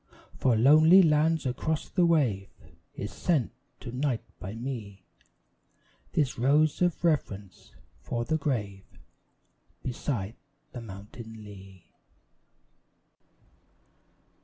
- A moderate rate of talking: No, slow, 95 wpm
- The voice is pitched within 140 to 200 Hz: No, low, 125 Hz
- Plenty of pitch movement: Yes, wide, 6.8 semitones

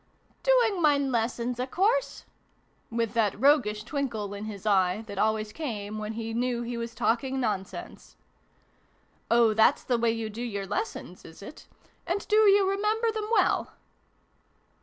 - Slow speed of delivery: No, average, 165 wpm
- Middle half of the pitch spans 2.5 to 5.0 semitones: No, wide, 5.5 semitones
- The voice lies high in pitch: Yes, high, 235 Hz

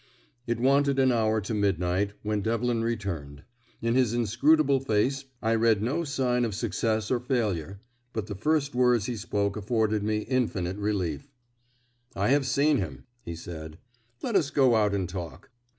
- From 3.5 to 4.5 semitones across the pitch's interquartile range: Yes, average, 4.2 semitones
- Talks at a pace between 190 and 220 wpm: No, average, 165 wpm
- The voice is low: Yes, low, 110 Hz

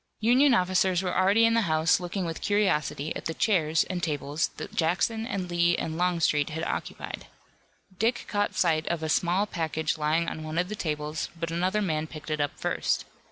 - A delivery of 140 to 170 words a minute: No, average, 195 wpm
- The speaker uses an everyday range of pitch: Yes, average, 3.5 semitones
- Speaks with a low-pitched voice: No, medium, 170 Hz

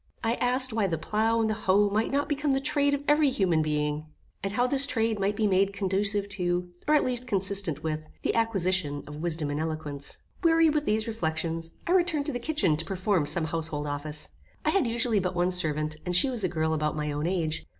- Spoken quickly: Yes, fast, 225 wpm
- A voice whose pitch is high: Yes, high, 195 Hz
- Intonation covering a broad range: Yes, wide, 7.0 semitones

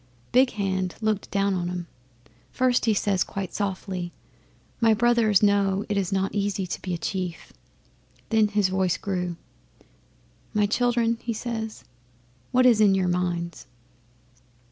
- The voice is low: No, high, 200 Hz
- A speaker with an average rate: Yes, average, 145 wpm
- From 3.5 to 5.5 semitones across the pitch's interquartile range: No, average, 2.9 semitones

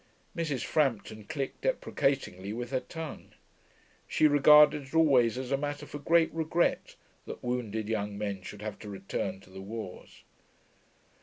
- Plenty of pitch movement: Yes, wide, 6.0 semitones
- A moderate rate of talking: Yes, average, 150 wpm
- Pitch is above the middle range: No, low, 125 Hz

